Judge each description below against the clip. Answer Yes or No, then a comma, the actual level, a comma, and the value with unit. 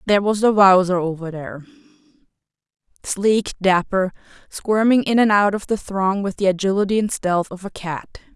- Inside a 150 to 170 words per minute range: Yes, average, 160 wpm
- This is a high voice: Yes, high, 195 Hz